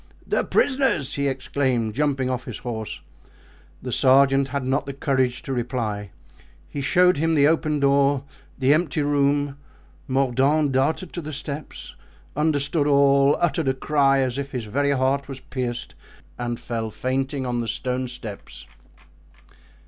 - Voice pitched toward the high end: No, low, 135 Hz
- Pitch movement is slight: Yes, narrow, 2.0 semitones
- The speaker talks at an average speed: Yes, average, 150 wpm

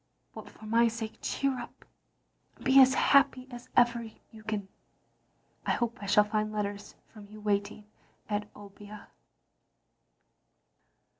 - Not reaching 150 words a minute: Yes, slow, 135 wpm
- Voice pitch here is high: Yes, high, 215 Hz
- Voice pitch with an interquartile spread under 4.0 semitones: Yes, narrow, 2.6 semitones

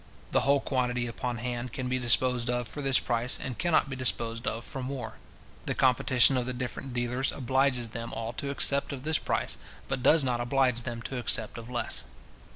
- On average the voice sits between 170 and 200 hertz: No, low, 125 Hz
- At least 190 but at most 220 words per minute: Yes, fast, 205 wpm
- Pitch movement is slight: Yes, narrow, 1.8 semitones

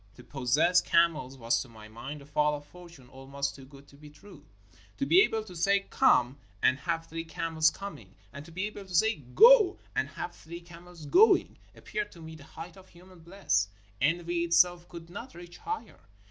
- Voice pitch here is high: No, medium, 165 Hz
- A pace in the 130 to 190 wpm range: No, average, 200 wpm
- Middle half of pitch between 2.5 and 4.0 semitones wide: No, average, 4.4 semitones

